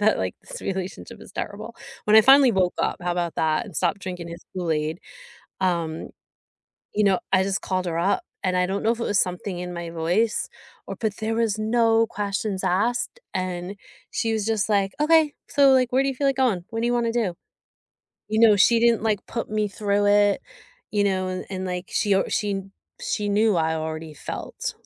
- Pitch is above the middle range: Yes, high, 200 Hz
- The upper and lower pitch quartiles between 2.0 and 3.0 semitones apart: No, average, 3.9 semitones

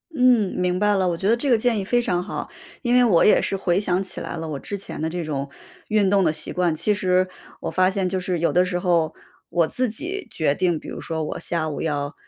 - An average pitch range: Yes, average, 3.8 semitones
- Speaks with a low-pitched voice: No, medium, 185 Hz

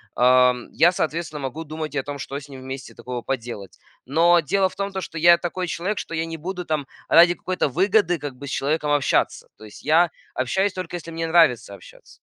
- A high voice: No, medium, 160 Hz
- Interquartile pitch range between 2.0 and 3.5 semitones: No, average, 4.5 semitones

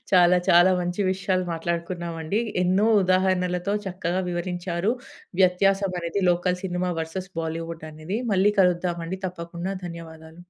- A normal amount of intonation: No, narrow, 1.6 semitones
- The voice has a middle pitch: Yes, medium, 180 Hz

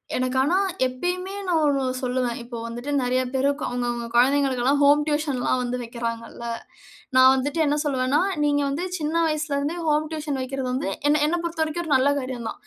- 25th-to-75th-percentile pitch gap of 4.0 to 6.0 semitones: No, average, 2.9 semitones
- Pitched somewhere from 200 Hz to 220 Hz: No, very high, 275 Hz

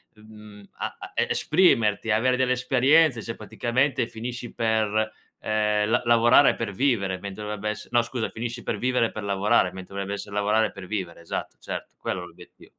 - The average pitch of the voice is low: Yes, low, 110 Hz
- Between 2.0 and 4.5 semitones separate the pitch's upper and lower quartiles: Yes, average, 2.7 semitones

